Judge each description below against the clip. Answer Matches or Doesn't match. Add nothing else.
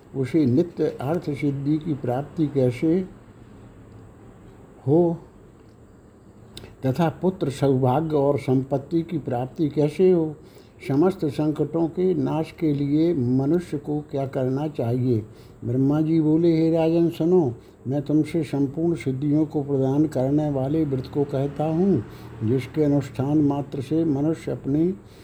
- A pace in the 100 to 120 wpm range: Matches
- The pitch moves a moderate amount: Matches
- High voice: Doesn't match